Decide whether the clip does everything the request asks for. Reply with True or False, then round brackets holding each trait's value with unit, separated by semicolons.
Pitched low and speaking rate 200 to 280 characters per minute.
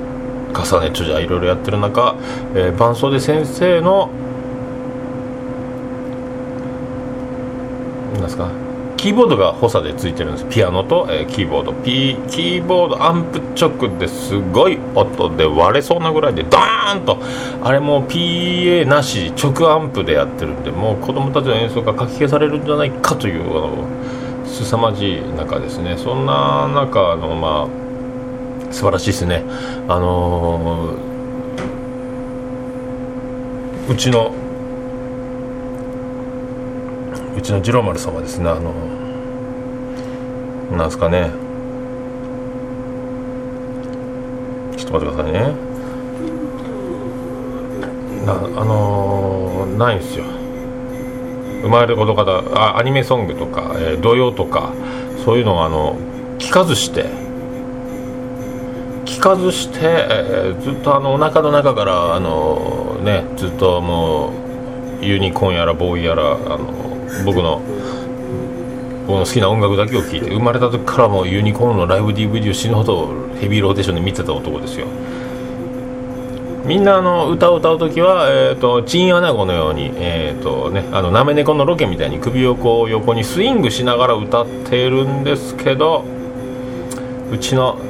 True (125 Hz; 265 characters per minute)